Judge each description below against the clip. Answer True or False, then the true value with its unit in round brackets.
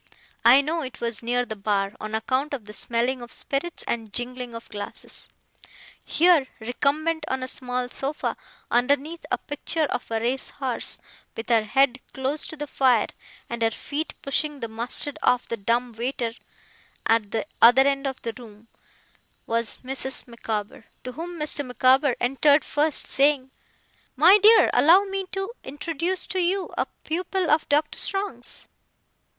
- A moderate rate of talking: True (160 wpm)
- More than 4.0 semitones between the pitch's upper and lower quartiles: True (4.4 semitones)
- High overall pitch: True (260 Hz)